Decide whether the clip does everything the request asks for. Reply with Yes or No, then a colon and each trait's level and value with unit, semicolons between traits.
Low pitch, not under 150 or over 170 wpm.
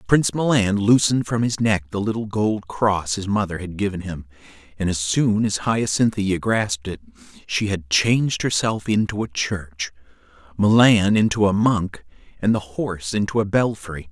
Yes: low, 100 Hz; average, 165 wpm